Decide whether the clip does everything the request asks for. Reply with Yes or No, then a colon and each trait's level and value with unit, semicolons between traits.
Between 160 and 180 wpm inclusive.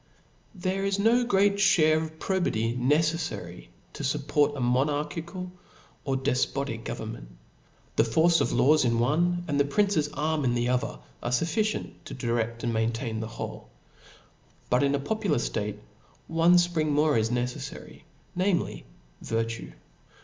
No: average, 145 wpm